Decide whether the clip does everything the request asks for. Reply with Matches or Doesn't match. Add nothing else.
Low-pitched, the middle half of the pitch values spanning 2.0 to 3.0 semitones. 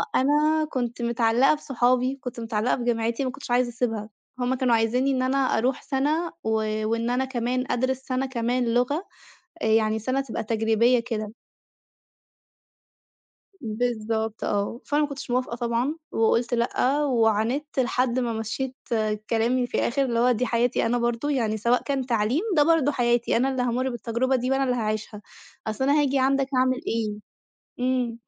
Doesn't match